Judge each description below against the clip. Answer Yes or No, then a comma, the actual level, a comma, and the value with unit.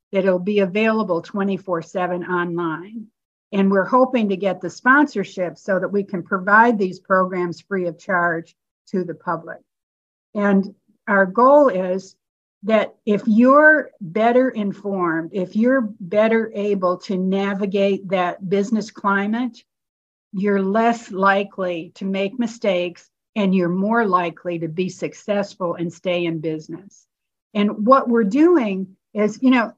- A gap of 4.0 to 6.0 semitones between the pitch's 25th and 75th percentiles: No, average, 3.2 semitones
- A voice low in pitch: No, high, 195 Hz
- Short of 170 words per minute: Yes, slow, 135 wpm